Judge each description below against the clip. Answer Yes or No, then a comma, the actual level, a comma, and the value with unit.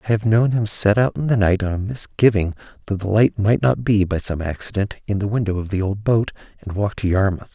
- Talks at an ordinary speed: No, fast, 255 wpm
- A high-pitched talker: No, low, 105 Hz